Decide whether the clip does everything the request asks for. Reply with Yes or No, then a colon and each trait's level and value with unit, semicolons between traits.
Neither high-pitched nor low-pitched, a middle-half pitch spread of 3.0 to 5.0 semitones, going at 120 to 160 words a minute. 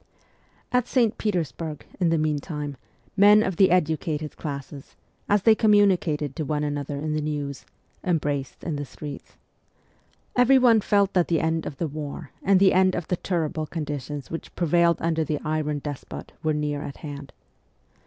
No: medium, 155 Hz; average, 3.9 semitones; average, 170 wpm